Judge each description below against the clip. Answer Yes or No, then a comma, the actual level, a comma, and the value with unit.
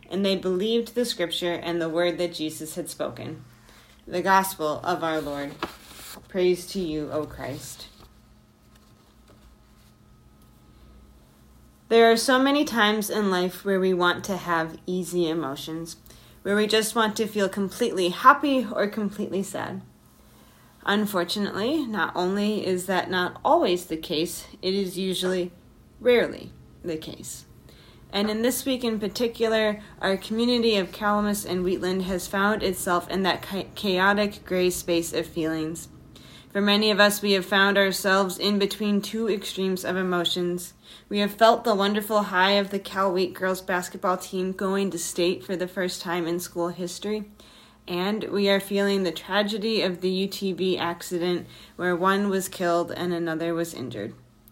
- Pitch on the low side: No, medium, 185 Hz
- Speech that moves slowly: No, average, 155 wpm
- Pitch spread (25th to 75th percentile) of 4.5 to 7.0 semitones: No, average, 2.8 semitones